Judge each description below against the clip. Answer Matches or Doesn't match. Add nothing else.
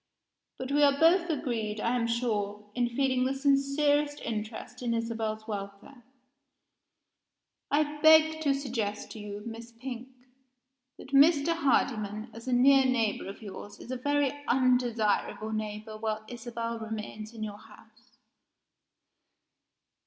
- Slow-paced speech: Matches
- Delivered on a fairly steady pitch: Doesn't match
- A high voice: Matches